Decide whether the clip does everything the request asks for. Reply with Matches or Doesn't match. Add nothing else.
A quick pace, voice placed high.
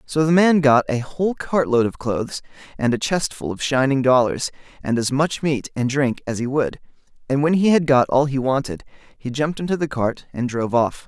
Doesn't match